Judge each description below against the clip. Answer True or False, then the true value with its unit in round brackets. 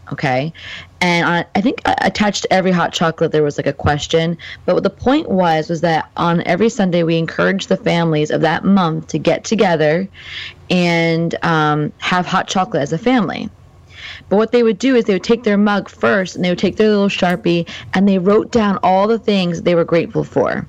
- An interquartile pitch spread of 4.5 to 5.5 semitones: False (3.6 semitones)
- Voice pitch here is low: False (175 Hz)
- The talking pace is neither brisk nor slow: False (210 wpm)